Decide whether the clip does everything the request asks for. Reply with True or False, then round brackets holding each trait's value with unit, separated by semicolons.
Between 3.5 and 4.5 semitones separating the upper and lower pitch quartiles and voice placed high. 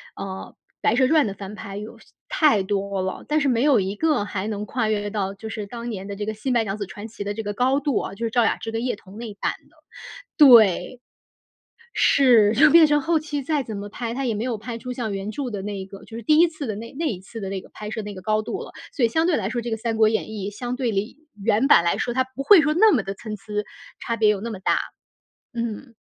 True (3.9 semitones; 225 Hz)